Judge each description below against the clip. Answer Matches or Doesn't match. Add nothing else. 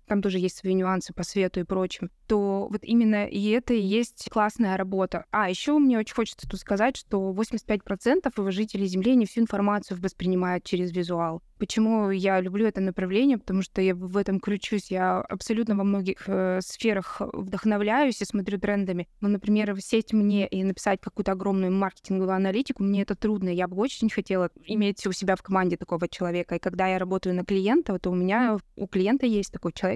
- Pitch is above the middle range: Matches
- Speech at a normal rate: Doesn't match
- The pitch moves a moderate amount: Doesn't match